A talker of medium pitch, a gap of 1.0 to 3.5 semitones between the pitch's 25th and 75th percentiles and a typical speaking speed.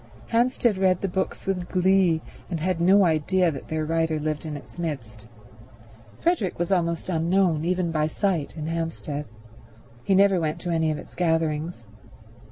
Yes: medium, 170 Hz; average, 3.2 semitones; average, 165 wpm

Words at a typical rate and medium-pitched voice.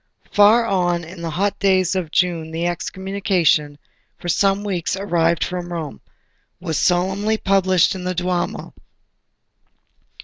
No: slow, 130 wpm; medium, 180 Hz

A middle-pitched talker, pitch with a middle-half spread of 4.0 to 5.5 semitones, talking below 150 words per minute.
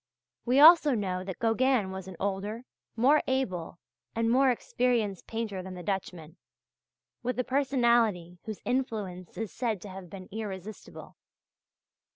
No: high, 215 Hz; average, 4.8 semitones; average, 140 wpm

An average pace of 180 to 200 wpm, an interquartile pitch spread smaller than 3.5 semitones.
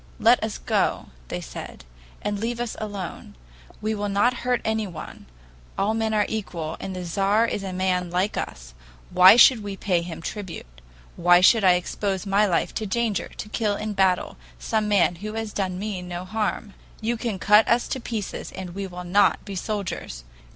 Yes: average, 185 wpm; average, 3.1 semitones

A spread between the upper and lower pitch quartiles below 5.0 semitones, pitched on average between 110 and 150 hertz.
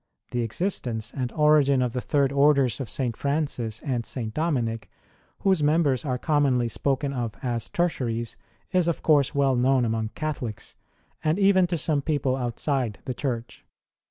Yes: average, 3.9 semitones; low, 135 Hz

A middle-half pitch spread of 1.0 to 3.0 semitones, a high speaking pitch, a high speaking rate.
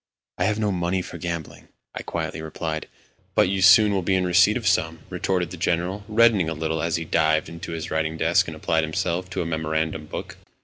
No: average, 2.7 semitones; very low, 85 Hz; fast, 215 wpm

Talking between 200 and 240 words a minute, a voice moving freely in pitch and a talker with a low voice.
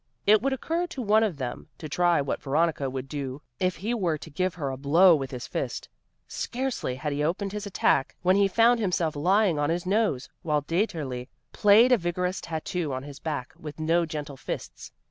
No: fast, 205 wpm; wide, 5.8 semitones; medium, 170 Hz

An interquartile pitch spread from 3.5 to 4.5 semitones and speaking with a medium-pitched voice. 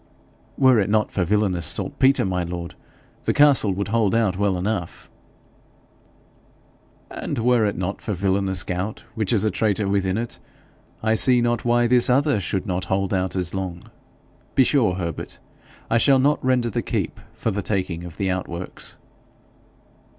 No: average, 4.1 semitones; low, 100 Hz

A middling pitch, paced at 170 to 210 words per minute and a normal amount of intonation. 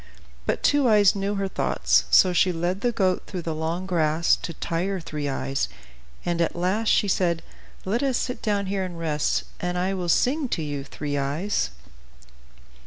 Yes: medium, 180 Hz; average, 180 wpm; average, 3.4 semitones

